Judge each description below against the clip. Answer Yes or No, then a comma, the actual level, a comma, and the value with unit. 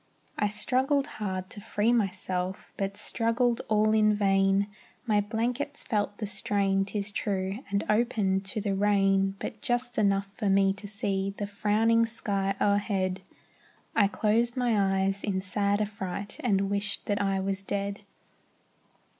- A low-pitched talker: No, high, 200 Hz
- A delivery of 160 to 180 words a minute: No, average, 145 wpm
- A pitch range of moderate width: No, narrow, 1.7 semitones